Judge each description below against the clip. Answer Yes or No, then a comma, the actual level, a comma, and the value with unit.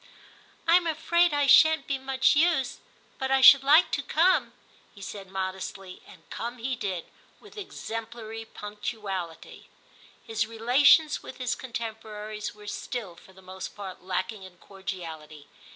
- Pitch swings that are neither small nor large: No, wide, 6.0 semitones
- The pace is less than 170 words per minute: Yes, average, 145 wpm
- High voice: Yes, high, 225 Hz